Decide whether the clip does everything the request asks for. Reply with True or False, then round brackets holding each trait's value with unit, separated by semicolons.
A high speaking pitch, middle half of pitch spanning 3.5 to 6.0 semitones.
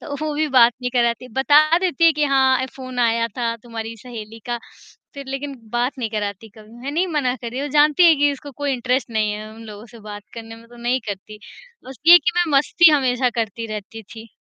True (245 Hz; 3.9 semitones)